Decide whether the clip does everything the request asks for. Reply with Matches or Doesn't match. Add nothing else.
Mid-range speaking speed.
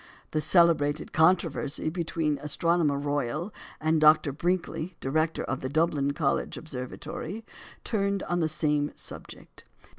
Doesn't match